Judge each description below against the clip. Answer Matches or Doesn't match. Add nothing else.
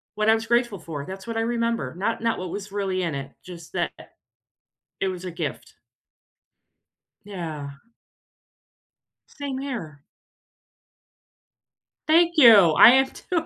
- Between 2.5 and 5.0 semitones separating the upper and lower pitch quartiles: Doesn't match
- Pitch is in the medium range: Doesn't match